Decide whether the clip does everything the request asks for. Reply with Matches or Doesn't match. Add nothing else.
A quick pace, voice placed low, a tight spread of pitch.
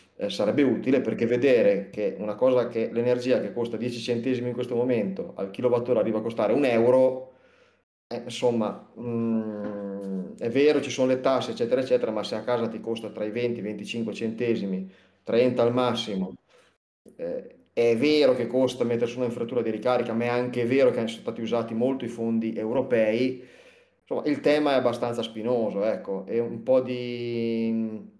Matches